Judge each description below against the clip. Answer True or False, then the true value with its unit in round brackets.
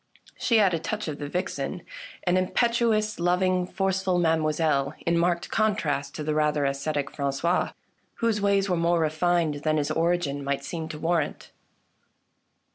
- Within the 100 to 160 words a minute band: True (150 wpm)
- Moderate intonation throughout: True (3.4 semitones)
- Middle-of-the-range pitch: True (170 Hz)